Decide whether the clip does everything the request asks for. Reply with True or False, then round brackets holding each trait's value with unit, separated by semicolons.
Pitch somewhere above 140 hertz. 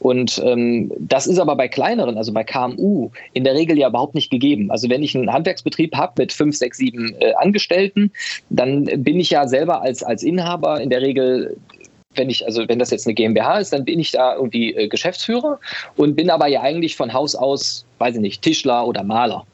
False (135 Hz)